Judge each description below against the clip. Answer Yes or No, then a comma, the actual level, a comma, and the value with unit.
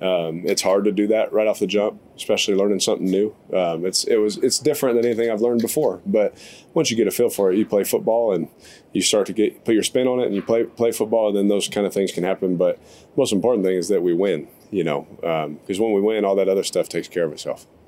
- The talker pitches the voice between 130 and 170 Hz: No, low, 110 Hz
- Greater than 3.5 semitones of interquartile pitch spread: Yes, average, 4.6 semitones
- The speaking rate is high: Yes, fast, 280 wpm